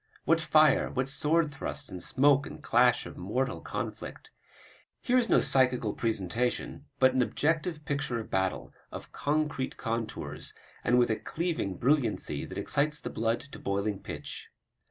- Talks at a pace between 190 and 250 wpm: No, average, 155 wpm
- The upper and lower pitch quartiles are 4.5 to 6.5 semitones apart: Yes, average, 4.8 semitones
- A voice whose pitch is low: Yes, low, 130 Hz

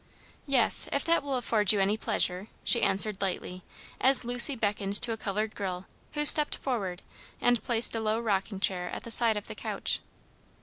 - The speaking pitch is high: Yes, high, 220 Hz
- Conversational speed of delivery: Yes, average, 185 wpm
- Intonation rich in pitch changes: No, average, 3.7 semitones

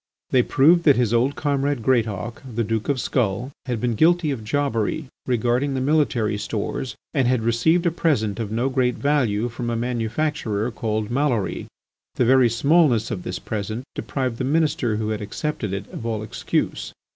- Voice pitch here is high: No, low, 120 Hz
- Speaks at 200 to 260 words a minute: No, average, 175 wpm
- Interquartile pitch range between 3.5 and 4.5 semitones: Yes, average, 4.2 semitones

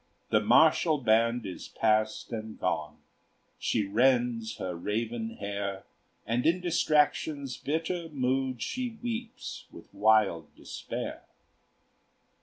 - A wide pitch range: Yes, wide, 5.7 semitones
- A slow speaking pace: Yes, slow, 105 wpm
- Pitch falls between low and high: No, low, 120 Hz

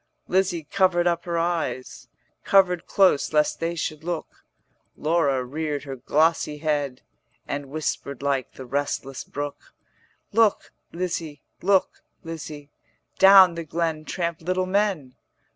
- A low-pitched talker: No, medium, 160 Hz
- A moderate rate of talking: No, slow, 125 wpm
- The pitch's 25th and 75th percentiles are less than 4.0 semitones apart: Yes, average, 3.5 semitones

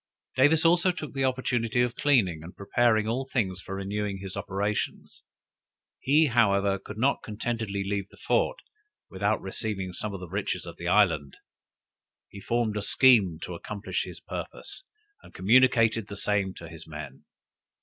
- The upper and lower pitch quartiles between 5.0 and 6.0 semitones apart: No, average, 4.0 semitones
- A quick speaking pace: No, average, 160 wpm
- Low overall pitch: Yes, low, 105 Hz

